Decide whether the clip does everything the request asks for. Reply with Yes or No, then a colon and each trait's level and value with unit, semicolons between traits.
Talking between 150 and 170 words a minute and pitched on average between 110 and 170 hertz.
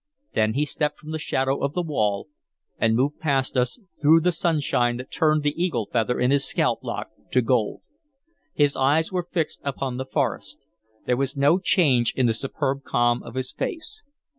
No: average, 190 wpm; low, 135 Hz